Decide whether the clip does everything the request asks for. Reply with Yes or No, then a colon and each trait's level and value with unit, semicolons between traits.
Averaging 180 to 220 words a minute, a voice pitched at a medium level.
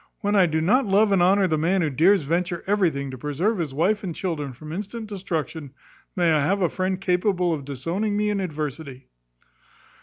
Yes: average, 195 wpm; medium, 175 Hz